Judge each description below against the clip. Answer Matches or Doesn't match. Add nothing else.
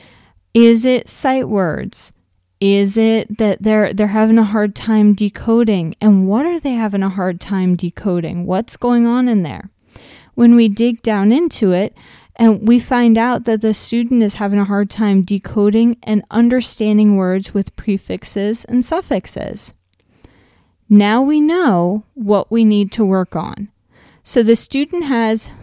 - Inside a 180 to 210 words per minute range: Doesn't match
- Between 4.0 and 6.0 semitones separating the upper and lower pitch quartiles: Doesn't match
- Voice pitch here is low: Doesn't match